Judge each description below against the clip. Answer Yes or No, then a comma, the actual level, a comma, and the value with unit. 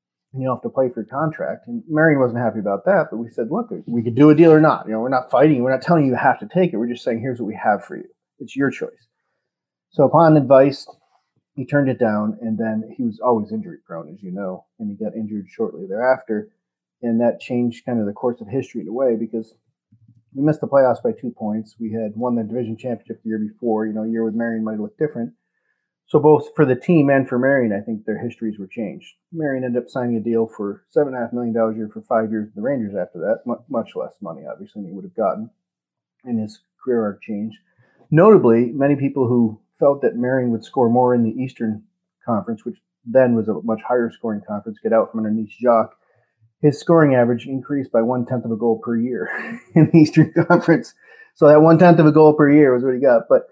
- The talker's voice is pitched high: No, low, 120 Hz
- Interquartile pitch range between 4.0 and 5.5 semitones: Yes, average, 4.6 semitones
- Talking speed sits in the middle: No, fast, 250 wpm